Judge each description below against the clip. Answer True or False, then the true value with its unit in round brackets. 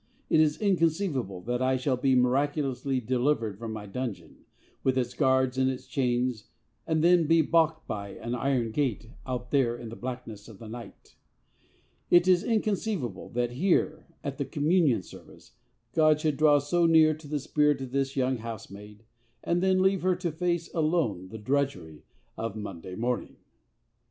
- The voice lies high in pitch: False (130 Hz)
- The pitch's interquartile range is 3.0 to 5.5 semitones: True (5.0 semitones)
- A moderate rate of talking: True (165 wpm)